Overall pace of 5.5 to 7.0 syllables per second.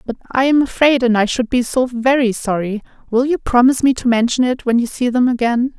Yes: 5.8 syllables/s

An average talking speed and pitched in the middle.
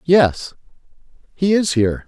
No: slow, 115 wpm; medium, 150 Hz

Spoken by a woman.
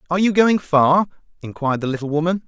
No: male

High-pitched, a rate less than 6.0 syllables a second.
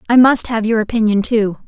Yes: high, 220 Hz; 5.6 syllables/s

